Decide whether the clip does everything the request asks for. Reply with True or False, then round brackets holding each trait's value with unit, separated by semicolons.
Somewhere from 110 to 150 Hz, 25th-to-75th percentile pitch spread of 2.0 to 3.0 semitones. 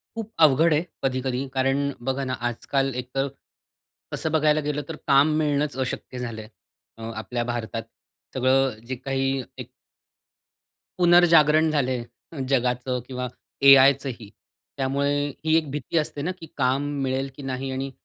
True (135 Hz; 2.6 semitones)